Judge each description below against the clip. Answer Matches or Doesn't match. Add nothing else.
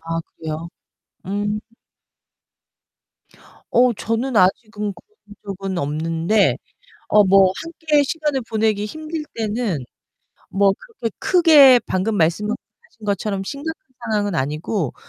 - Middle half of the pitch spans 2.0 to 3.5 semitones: Doesn't match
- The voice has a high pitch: Matches